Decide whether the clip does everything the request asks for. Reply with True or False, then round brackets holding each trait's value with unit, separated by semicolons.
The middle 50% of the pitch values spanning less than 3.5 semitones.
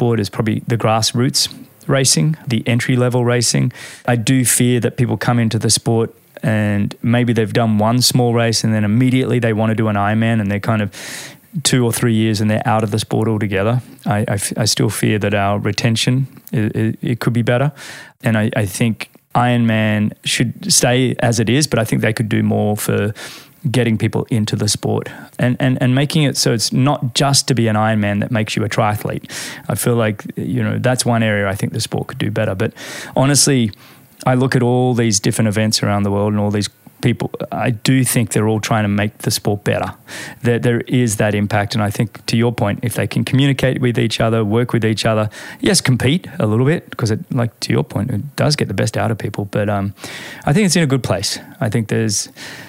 True (2.7 semitones)